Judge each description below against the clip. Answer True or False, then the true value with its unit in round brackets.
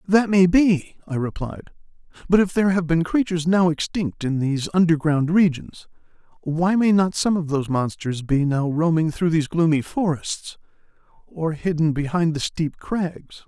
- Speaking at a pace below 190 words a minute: True (165 wpm)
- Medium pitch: True (165 Hz)